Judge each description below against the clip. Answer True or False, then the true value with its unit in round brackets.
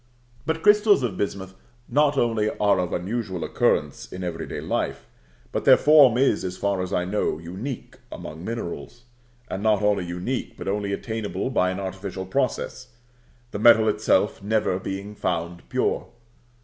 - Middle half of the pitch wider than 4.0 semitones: True (4.4 semitones)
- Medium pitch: False (100 Hz)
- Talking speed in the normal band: True (160 wpm)